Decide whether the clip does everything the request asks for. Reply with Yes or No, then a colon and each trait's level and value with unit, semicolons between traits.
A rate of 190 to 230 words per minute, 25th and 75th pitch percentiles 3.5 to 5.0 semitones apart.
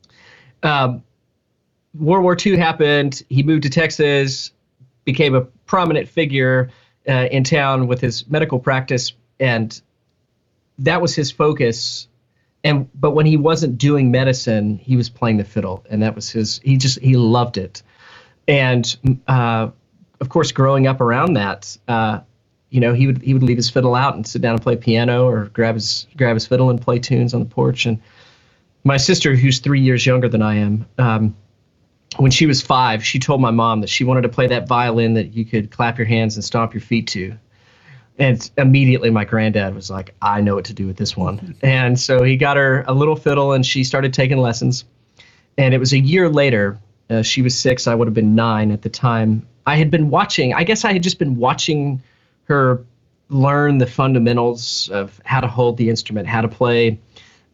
No: average, 195 wpm; average, 3.0 semitones